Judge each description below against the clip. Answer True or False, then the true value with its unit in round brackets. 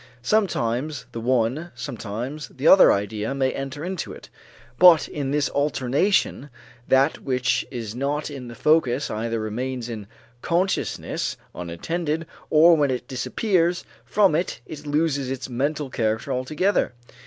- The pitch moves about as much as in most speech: True (4.4 semitones)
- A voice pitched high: False (135 Hz)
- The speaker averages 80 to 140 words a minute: True (135 wpm)